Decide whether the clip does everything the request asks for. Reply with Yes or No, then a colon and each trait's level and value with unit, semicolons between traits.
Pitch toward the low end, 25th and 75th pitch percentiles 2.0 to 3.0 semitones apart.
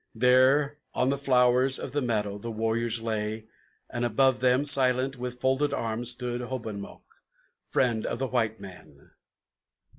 Yes: low, 125 Hz; average, 2.7 semitones